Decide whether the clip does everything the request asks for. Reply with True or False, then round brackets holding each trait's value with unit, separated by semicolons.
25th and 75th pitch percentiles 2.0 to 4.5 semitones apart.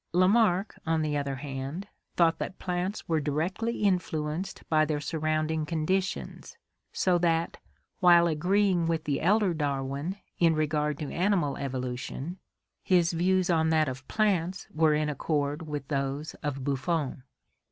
True (3.4 semitones)